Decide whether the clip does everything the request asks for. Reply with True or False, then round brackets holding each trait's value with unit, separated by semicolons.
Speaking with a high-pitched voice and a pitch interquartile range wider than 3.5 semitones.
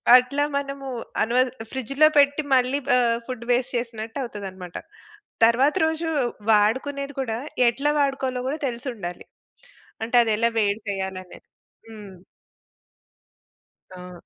True (240 Hz; 4.4 semitones)